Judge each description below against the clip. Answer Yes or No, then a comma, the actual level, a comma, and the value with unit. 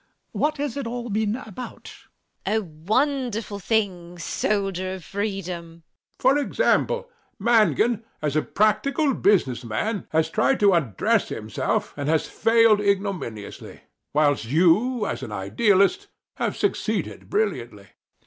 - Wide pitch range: Yes, wide, 5.9 semitones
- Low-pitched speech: No, high, 200 Hz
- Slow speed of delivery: Yes, slow, 130 wpm